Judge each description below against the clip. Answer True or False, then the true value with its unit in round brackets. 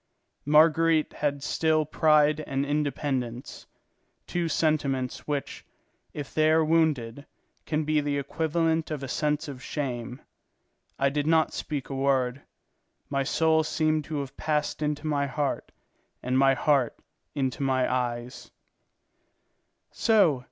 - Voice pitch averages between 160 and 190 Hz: False (145 Hz)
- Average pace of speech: False (125 wpm)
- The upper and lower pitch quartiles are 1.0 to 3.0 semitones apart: True (2.4 semitones)